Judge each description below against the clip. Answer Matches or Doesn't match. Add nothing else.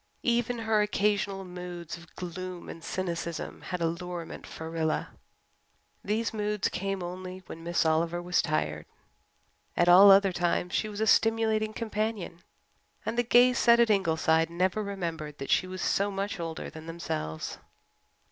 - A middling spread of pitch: Matches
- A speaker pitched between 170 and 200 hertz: Matches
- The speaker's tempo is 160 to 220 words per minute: Doesn't match